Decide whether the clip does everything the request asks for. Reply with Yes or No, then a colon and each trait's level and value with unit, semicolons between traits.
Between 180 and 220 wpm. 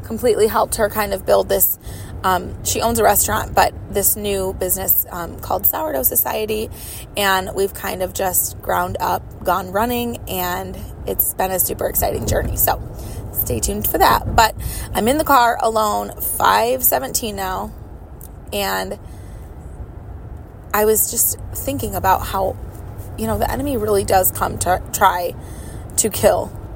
No: average, 150 wpm